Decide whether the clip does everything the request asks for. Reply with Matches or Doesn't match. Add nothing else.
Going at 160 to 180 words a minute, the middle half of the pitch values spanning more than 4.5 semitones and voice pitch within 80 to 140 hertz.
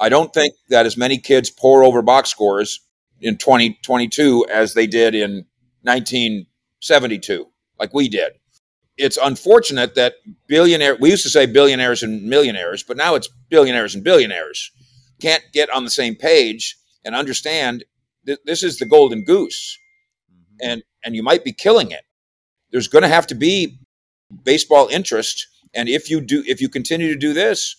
Matches